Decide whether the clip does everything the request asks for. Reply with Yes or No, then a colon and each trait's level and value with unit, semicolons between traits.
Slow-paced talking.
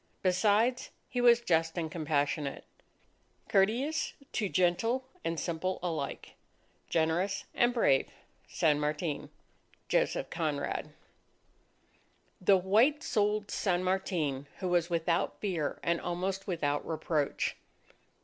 Yes: slow, 105 wpm